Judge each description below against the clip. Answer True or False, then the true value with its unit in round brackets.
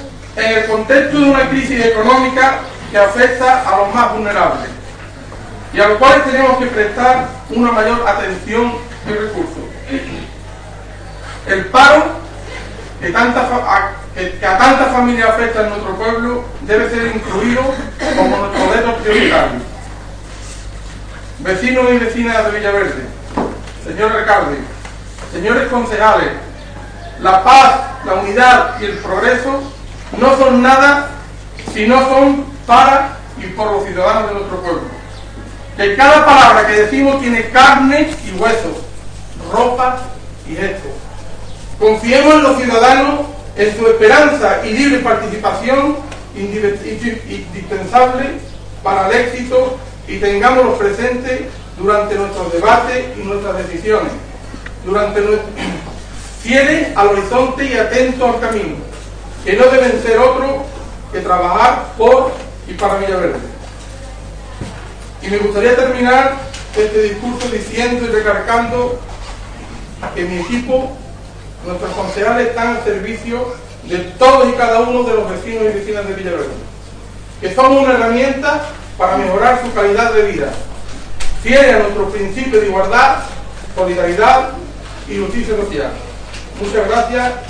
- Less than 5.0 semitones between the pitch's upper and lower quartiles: False (5.3 semitones)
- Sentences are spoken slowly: True (125 wpm)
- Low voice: False (215 Hz)